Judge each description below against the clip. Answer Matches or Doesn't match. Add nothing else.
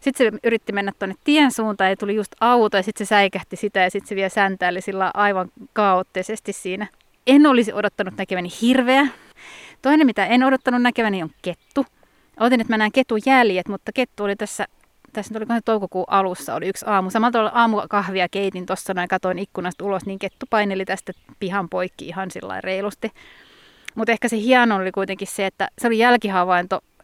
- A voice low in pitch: Doesn't match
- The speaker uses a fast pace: Matches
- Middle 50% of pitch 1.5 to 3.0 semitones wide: Doesn't match